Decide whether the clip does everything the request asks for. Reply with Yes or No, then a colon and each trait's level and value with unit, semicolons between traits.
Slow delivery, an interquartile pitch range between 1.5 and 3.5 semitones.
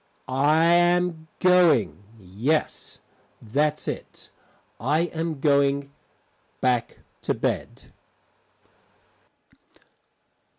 No: slow, 70 wpm; average, 4.3 semitones